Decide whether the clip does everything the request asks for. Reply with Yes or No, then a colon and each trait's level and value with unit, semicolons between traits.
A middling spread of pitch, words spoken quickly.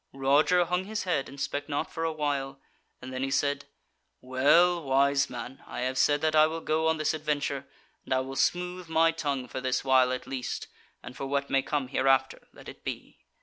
Yes: average, 3.1 semitones; fast, 210 wpm